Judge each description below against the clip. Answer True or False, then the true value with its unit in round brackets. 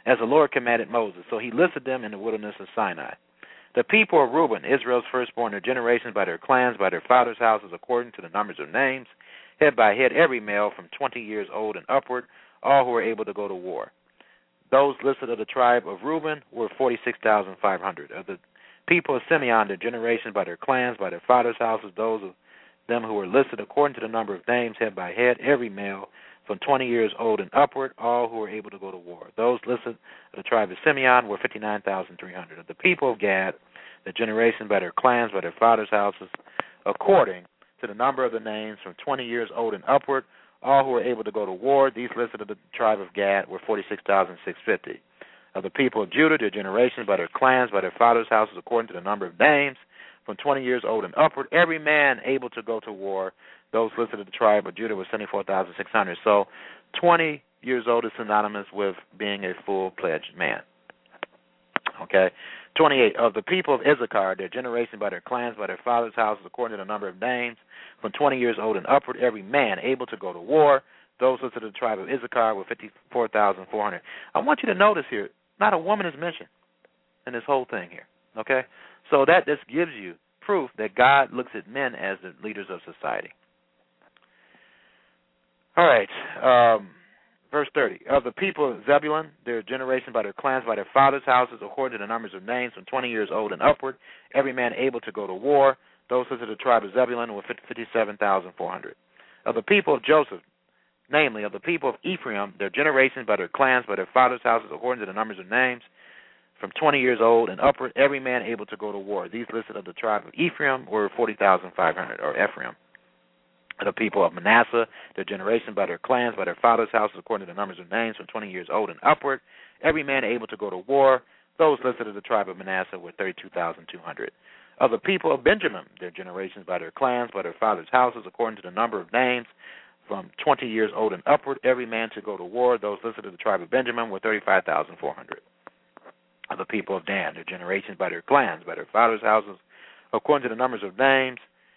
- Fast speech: True (210 wpm)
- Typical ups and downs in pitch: True (3.8 semitones)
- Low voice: True (120 Hz)